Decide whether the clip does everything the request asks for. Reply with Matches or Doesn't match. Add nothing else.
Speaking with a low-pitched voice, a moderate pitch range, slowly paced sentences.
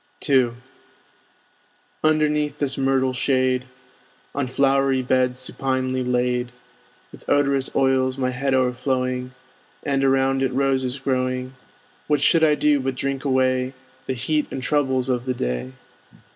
Doesn't match